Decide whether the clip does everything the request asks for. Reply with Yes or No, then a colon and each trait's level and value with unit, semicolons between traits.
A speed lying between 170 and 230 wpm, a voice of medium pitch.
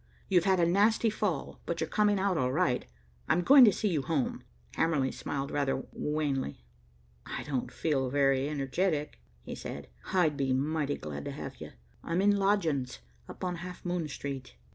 Yes: average, 175 wpm; medium, 155 Hz